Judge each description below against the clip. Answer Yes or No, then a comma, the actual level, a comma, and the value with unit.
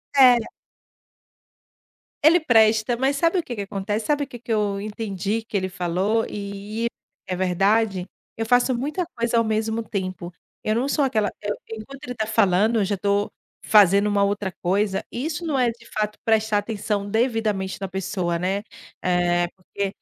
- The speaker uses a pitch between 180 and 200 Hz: No, high, 215 Hz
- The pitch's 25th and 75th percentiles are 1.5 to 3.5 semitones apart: Yes, average, 2.9 semitones